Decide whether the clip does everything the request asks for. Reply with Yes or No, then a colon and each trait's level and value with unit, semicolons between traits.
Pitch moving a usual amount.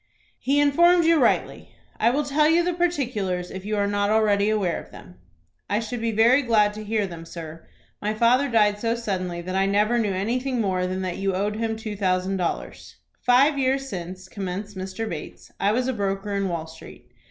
Yes: average, 4.4 semitones